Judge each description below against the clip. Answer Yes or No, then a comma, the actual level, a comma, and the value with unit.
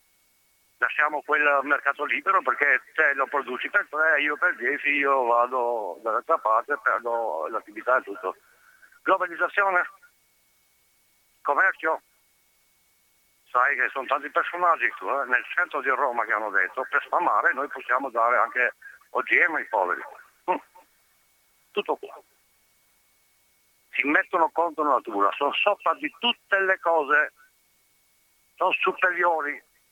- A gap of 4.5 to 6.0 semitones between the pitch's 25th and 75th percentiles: Yes, average, 5.3 semitones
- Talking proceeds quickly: No, average, 125 wpm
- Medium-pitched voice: Yes, medium, 150 Hz